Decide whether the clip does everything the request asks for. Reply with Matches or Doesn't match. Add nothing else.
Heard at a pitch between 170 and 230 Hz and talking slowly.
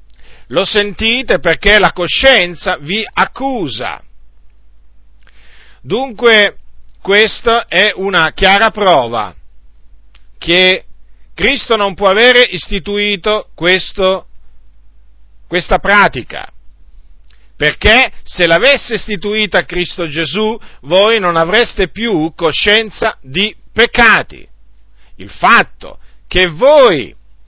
Matches